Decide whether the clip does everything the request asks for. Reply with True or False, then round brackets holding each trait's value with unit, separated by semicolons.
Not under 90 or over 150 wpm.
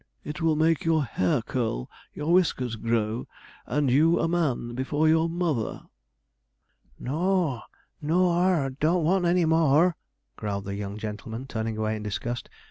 False (160 wpm)